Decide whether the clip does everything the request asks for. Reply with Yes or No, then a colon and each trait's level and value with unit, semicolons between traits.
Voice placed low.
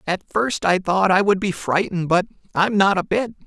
No: high, 190 Hz